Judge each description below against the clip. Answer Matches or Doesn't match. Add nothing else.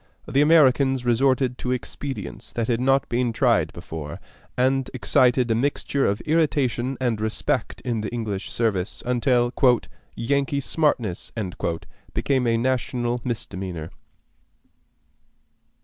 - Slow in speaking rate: Matches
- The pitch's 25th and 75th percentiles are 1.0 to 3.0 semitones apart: Matches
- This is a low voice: Matches